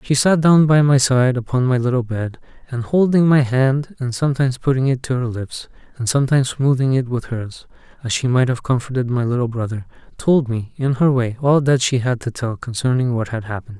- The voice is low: Yes, low, 130 Hz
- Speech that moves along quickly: Yes, fast, 215 wpm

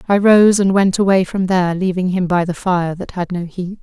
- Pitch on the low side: No, medium, 185 Hz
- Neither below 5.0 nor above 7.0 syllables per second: Yes, 5.2 syllables/s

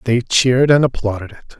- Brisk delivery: No, average, 190 wpm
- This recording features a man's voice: Yes, male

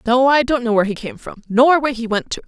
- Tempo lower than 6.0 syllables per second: No, 6.6 syllables/s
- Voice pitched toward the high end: Yes, high, 245 Hz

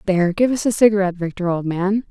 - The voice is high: Yes, high, 195 Hz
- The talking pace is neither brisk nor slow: No, fast, 230 wpm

